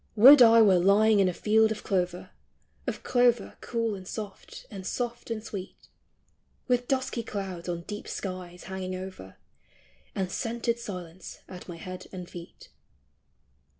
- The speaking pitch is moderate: No, high, 195 Hz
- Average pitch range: Yes, average, 3.8 semitones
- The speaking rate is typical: Yes, average, 150 wpm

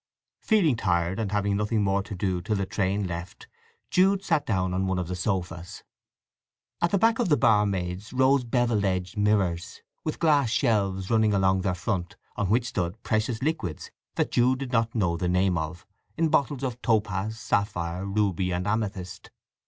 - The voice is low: Yes, low, 100 Hz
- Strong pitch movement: No, average, 4.3 semitones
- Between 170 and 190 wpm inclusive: Yes, average, 175 wpm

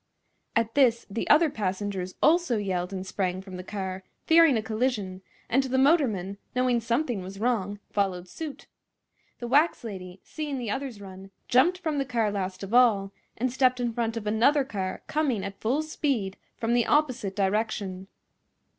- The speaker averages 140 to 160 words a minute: No, average, 170 wpm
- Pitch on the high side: Yes, high, 225 Hz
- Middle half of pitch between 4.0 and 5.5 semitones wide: Yes, average, 5.2 semitones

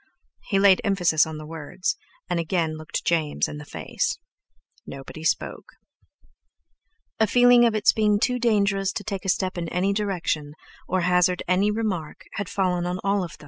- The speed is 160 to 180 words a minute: Yes, average, 170 wpm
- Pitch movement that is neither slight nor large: Yes, average, 3.5 semitones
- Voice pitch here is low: No, medium, 185 Hz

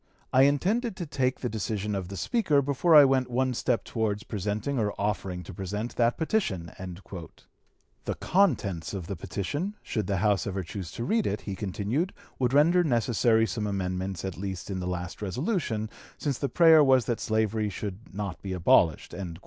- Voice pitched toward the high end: No, low, 110 Hz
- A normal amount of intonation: No, wide, 6.1 semitones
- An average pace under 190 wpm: Yes, average, 180 wpm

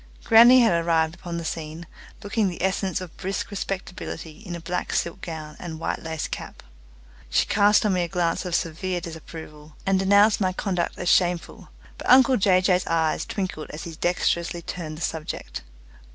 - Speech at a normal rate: Yes, average, 180 wpm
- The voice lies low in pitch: No, medium, 175 Hz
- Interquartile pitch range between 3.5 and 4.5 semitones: No, average, 2.9 semitones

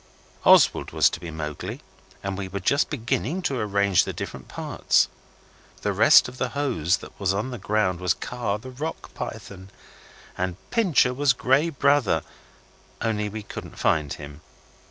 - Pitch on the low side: Yes, low, 105 Hz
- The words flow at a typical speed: Yes, average, 160 wpm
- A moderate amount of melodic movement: No, wide, 6.0 semitones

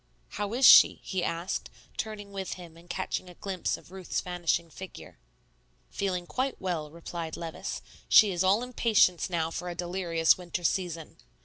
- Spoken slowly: No, average, 165 wpm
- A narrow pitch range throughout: Yes, narrow, 2.3 semitones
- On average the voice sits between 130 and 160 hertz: No, medium, 180 Hz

